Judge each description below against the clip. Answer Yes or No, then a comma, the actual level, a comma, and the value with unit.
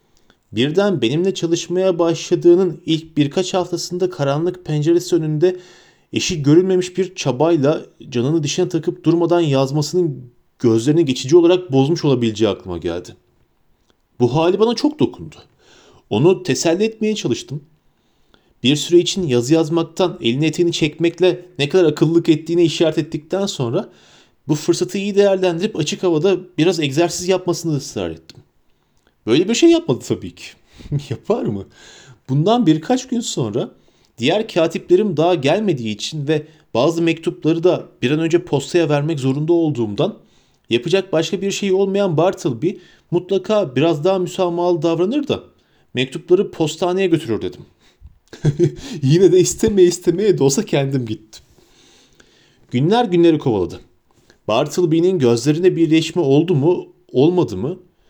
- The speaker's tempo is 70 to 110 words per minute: No, average, 130 wpm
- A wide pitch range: No, average, 3.5 semitones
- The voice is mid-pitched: Yes, medium, 170 Hz